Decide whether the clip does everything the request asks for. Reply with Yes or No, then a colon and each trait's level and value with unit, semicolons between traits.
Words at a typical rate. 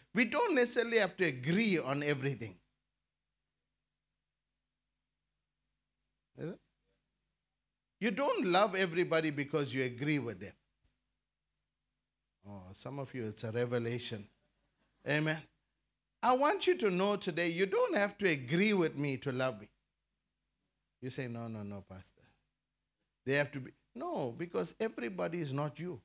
No: slow, 130 wpm